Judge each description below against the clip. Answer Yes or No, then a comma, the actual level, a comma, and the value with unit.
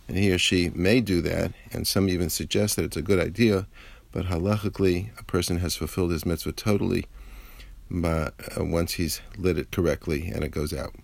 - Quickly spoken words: No, average, 195 wpm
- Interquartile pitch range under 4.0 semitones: Yes, average, 3.4 semitones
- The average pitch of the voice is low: Yes, very low, 90 Hz